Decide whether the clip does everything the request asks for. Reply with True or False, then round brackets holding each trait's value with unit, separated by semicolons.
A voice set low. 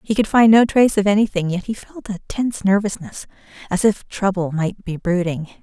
False (195 Hz)